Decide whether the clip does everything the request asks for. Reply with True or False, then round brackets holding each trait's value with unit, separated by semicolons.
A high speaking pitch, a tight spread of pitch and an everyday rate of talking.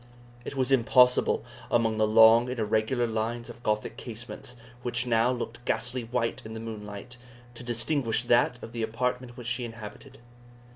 False (120 Hz; 1.8 semitones; 160 wpm)